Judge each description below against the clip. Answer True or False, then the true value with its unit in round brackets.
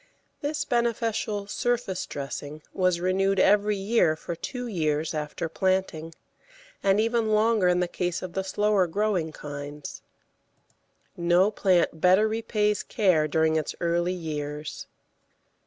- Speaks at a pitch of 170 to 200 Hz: True (185 Hz)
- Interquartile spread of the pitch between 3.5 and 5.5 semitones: True (4.7 semitones)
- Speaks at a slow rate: True (125 wpm)